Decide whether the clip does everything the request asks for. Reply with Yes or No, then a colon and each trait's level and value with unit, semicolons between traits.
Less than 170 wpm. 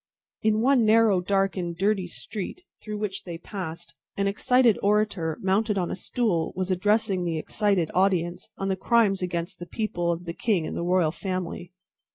No: average, 180 wpm